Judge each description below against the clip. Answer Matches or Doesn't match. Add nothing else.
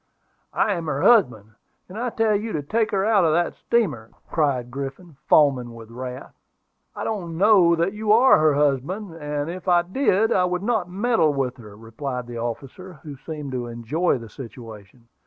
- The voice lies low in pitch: Doesn't match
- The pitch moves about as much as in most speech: Doesn't match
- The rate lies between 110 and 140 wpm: Doesn't match